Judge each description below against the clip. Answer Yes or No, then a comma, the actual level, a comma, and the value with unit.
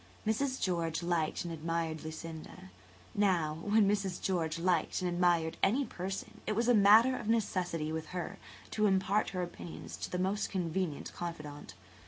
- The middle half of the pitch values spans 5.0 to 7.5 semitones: No, average, 3.6 semitones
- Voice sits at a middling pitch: Yes, medium, 180 Hz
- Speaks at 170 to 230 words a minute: No, average, 160 wpm